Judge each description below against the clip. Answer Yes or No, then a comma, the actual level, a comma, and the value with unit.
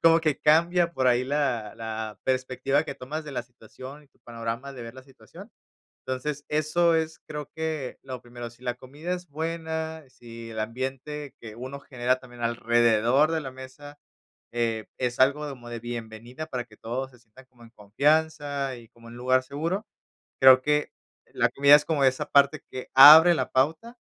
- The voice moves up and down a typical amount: Yes, average, 3.9 semitones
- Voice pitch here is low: Yes, low, 130 Hz